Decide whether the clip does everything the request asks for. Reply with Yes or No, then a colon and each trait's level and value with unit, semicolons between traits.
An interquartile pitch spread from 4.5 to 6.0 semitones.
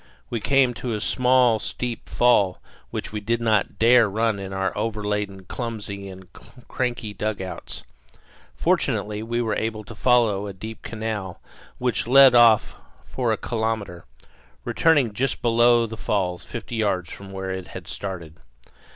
No: average, 3.0 semitones